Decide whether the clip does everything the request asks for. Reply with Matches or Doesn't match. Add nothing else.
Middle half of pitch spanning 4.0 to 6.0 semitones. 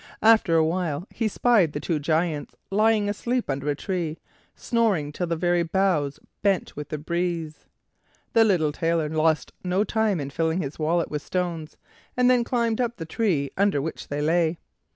Matches